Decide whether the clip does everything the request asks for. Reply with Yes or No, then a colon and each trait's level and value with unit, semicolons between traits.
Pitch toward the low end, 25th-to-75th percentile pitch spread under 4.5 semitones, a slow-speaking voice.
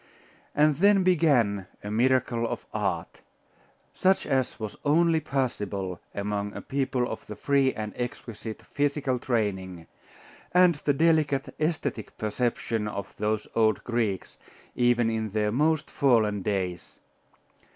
No: low, 120 Hz; average, 5.2 semitones; slow, 125 wpm